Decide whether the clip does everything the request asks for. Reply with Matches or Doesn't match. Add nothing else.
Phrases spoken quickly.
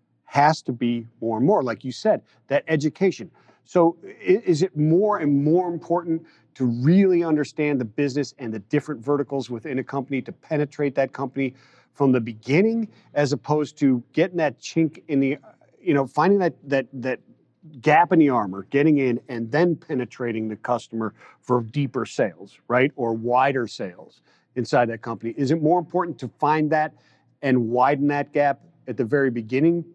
Doesn't match